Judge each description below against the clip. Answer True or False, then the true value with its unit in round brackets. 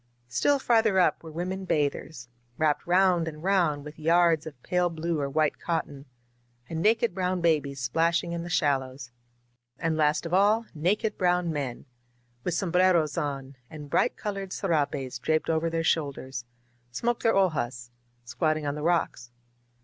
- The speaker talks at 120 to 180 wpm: True (155 wpm)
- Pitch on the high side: False (160 Hz)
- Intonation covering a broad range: False (3.7 semitones)